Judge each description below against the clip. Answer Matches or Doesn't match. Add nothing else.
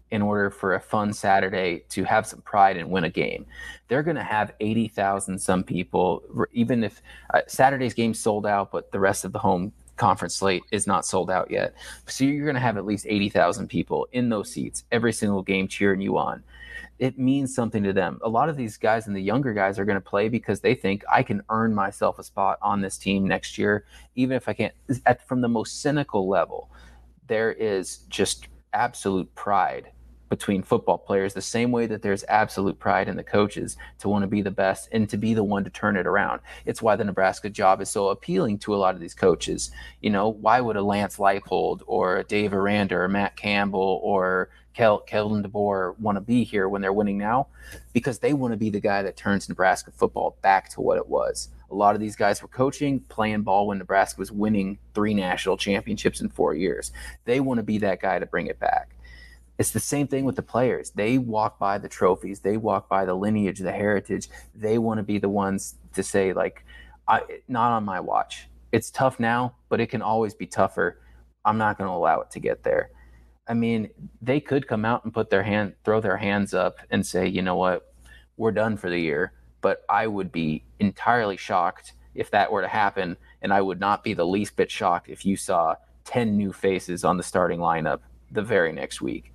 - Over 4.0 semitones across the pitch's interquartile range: Doesn't match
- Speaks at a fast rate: Matches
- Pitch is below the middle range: Matches